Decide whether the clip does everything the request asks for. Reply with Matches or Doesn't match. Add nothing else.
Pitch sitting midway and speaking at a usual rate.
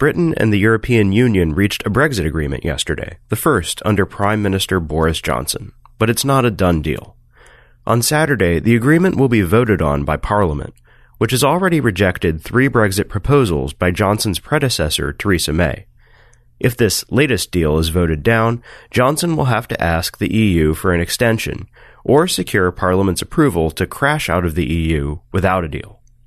Doesn't match